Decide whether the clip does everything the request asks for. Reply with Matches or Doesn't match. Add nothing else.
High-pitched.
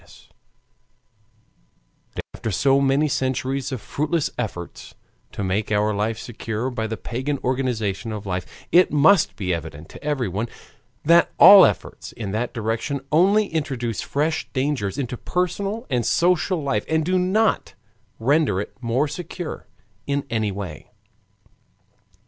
Doesn't match